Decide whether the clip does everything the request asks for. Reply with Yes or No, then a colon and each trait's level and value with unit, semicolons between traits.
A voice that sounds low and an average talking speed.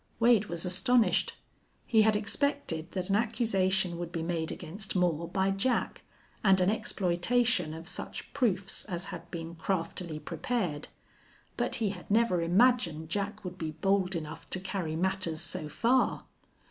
No: medium, 185 Hz; average, 150 wpm